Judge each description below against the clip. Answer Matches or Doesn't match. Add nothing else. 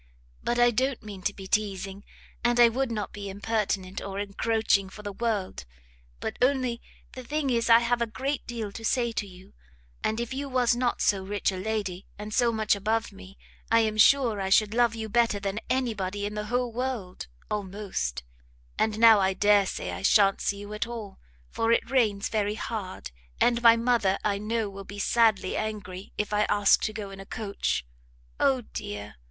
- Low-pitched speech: Doesn't match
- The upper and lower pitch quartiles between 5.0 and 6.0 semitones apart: Doesn't match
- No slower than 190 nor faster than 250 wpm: Matches